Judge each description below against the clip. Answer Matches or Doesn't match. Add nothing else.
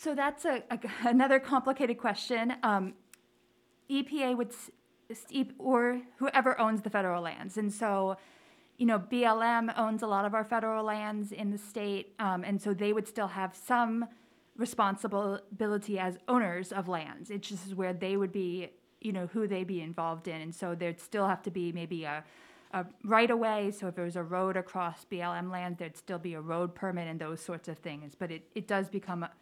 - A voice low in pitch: Doesn't match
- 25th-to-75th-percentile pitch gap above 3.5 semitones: Matches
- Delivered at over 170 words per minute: Matches